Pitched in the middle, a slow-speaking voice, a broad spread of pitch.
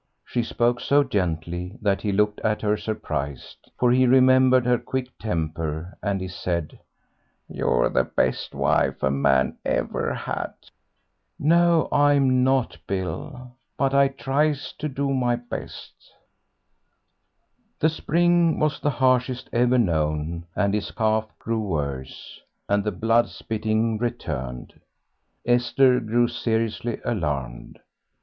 No: low, 115 Hz; slow, 125 wpm; wide, 6.2 semitones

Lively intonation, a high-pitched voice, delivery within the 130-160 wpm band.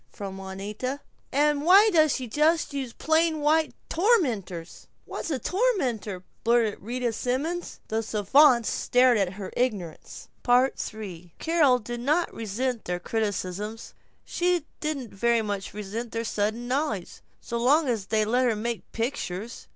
Yes: wide, 5.7 semitones; high, 240 Hz; average, 140 wpm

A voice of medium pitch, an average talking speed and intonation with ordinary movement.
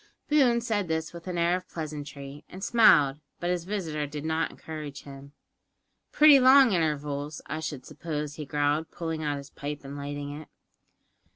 Yes: medium, 155 Hz; average, 170 wpm; average, 3.4 semitones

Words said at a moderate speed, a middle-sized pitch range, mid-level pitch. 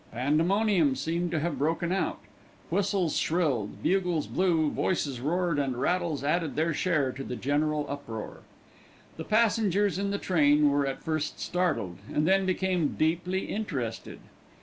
Yes: average, 145 wpm; average, 4.3 semitones; medium, 160 Hz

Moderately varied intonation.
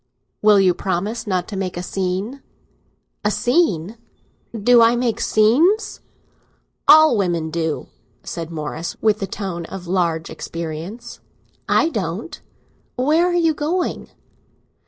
No: wide, 5.7 semitones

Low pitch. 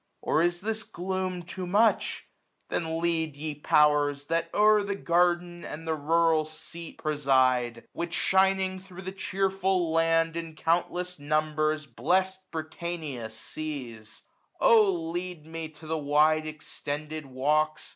No: medium, 165 Hz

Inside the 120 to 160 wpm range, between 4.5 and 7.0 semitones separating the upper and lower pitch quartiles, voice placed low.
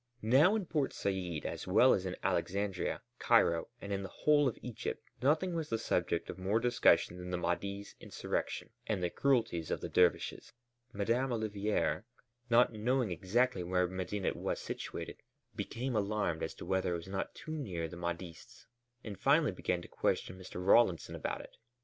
No: average, 175 wpm; average, 5.1 semitones; low, 100 Hz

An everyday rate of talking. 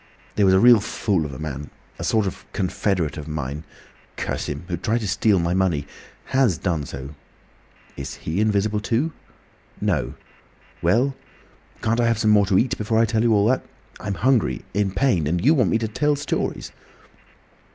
Yes: average, 170 wpm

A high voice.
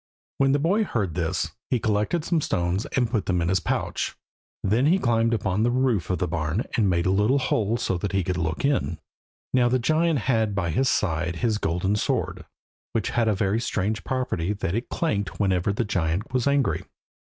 No: low, 105 Hz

